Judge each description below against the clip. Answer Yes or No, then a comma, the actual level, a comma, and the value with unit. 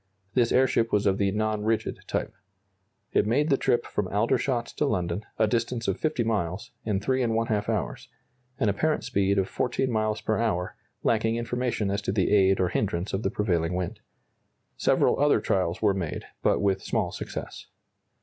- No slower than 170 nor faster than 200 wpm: Yes, average, 175 wpm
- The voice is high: No, low, 105 Hz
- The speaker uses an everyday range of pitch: Yes, average, 3.1 semitones